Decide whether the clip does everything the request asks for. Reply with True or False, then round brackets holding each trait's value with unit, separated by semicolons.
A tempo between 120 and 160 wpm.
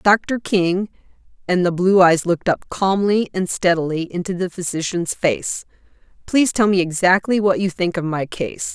False (170 wpm)